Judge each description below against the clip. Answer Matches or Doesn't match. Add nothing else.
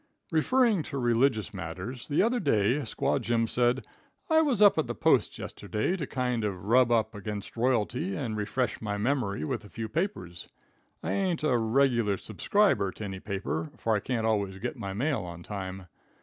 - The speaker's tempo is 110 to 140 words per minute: Doesn't match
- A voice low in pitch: Matches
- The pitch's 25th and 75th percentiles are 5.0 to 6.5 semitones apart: Matches